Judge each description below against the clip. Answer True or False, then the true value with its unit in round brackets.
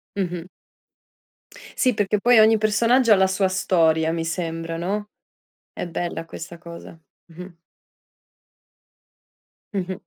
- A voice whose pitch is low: False (185 Hz)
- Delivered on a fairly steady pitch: False (3.8 semitones)